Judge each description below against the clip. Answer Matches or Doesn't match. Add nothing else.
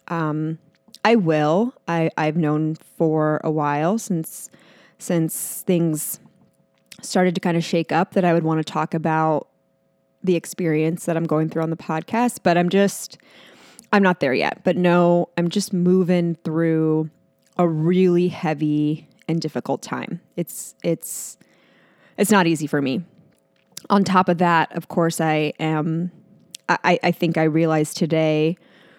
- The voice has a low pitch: Doesn't match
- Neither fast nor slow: Matches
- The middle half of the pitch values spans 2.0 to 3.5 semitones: Matches